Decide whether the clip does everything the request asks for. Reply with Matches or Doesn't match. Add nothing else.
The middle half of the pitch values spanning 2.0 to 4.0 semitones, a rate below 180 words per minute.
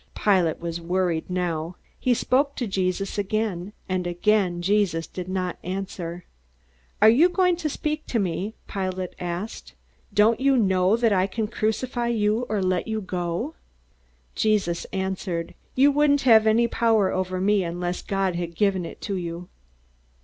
Matches